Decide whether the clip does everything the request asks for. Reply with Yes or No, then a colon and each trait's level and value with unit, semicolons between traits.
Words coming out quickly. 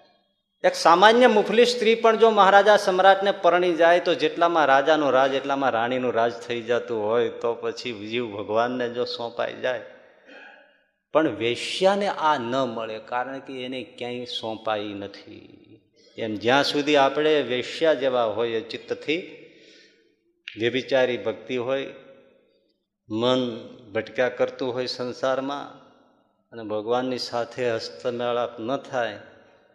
No: average, 120 wpm